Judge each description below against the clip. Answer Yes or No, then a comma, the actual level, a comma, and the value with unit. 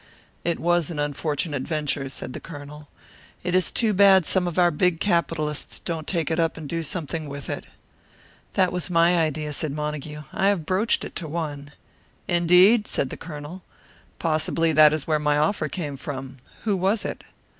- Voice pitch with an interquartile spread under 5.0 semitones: Yes, average, 3.0 semitones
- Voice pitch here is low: No, medium, 160 Hz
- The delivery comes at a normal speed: Yes, average, 180 wpm